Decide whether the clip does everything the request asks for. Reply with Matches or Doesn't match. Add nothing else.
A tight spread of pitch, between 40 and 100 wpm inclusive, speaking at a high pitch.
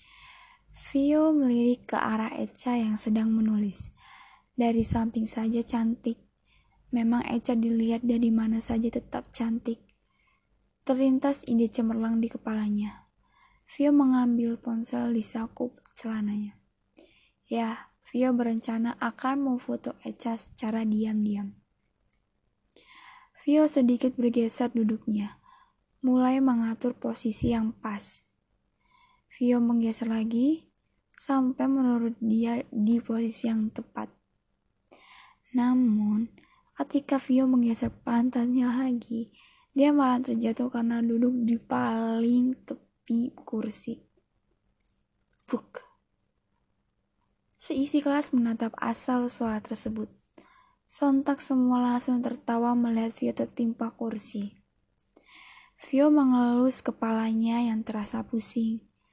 Matches